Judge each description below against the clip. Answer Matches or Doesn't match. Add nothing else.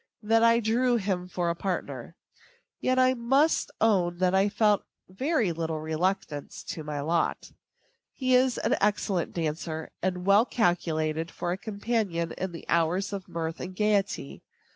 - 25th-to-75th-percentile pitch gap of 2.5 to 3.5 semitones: Doesn't match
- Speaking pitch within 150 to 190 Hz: Matches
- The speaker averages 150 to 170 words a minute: Matches